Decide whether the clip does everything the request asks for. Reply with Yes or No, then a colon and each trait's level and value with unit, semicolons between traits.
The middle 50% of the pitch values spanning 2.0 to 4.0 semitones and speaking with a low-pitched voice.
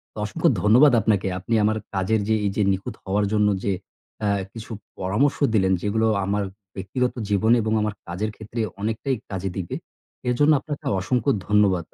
Yes: narrow, 2.6 semitones; low, 105 Hz